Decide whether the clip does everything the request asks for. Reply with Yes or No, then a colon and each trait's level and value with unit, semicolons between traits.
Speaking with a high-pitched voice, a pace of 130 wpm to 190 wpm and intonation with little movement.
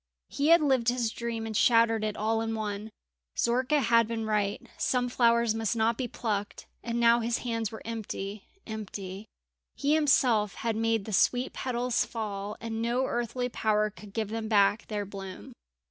Yes: high, 225 Hz; average, 175 wpm; narrow, 2.0 semitones